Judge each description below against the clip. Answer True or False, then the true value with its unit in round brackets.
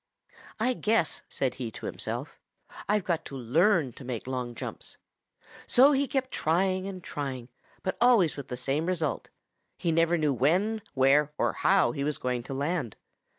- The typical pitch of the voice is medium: True (155 Hz)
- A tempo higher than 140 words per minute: True (170 wpm)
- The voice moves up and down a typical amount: False (6.2 semitones)